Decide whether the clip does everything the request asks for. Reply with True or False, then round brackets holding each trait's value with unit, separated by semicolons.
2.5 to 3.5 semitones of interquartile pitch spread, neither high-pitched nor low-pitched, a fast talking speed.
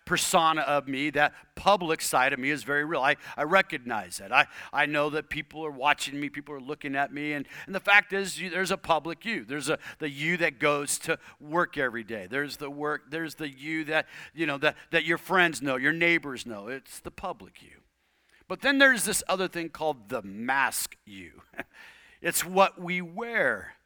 True (3.1 semitones; 155 Hz; 210 wpm)